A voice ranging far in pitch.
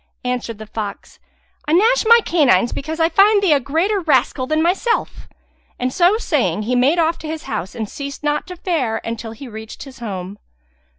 Yes: wide, 7.0 semitones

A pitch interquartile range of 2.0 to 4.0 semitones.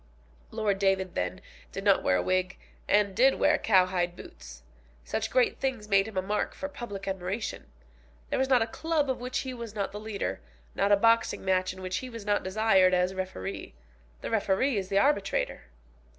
Yes: average, 3.7 semitones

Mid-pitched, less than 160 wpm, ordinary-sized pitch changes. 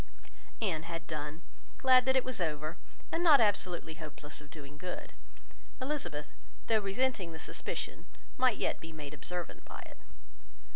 No: medium, 170 Hz; average, 150 wpm; wide, 8.0 semitones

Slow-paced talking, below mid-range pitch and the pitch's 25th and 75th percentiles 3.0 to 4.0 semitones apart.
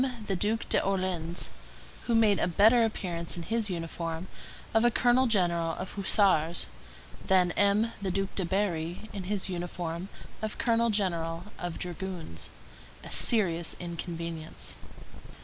No: slow, 130 wpm; medium, 185 Hz; average, 3.6 semitones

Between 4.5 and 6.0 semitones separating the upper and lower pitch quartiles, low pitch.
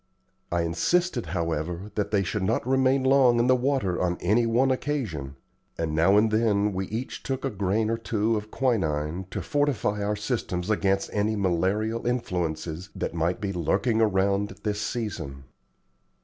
Yes: average, 4.8 semitones; low, 105 Hz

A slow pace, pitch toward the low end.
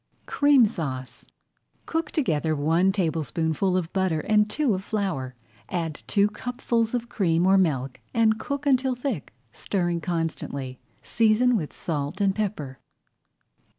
No: slow, 130 wpm; high, 190 Hz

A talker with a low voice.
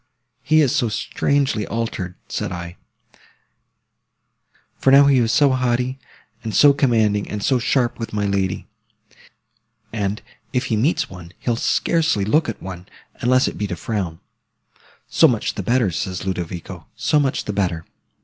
Yes: low, 115 Hz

